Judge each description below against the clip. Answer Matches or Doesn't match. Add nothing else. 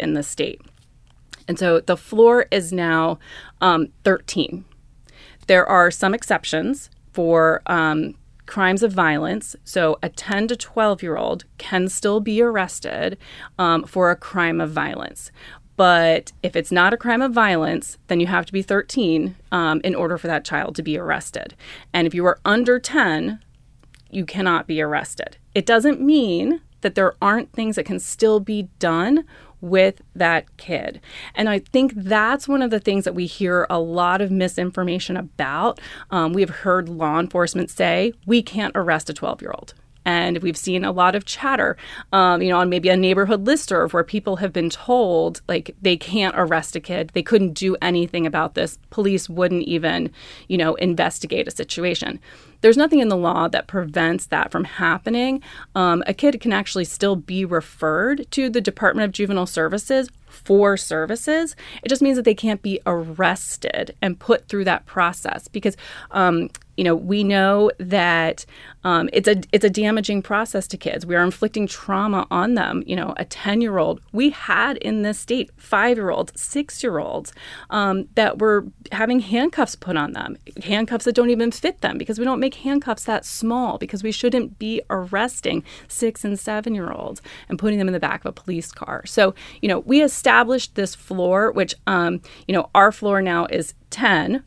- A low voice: Doesn't match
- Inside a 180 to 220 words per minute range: Matches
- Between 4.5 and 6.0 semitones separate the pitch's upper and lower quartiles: Doesn't match